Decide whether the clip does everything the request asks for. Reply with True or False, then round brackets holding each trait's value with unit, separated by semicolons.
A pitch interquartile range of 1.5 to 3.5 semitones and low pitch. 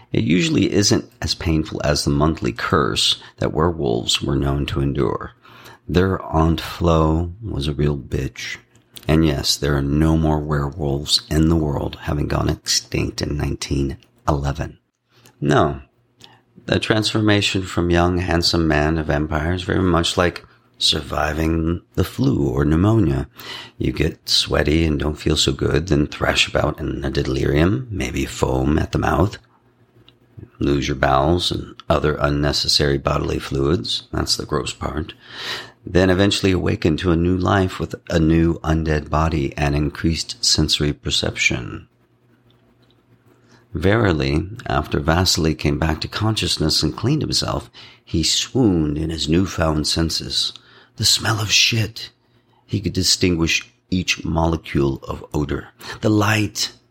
False (4.3 semitones; 80 Hz)